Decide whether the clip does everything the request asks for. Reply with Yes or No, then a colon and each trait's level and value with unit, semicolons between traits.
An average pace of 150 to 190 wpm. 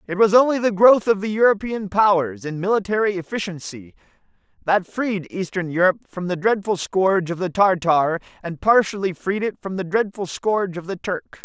Yes: average, 180 wpm